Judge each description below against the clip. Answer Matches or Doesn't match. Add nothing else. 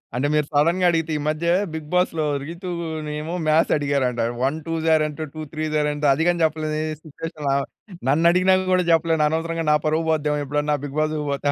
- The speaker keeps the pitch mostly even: Matches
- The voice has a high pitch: Doesn't match